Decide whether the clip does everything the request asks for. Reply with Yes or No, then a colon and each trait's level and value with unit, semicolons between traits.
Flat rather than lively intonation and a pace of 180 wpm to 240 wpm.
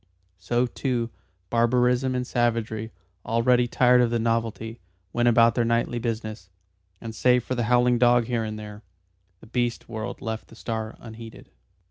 No: narrow, 1.5 semitones; average, 155 wpm